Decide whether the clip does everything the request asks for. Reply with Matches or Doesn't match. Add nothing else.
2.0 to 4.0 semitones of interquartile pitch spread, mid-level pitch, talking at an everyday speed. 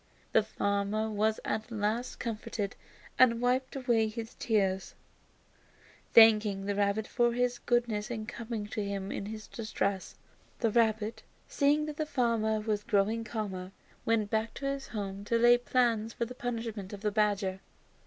Doesn't match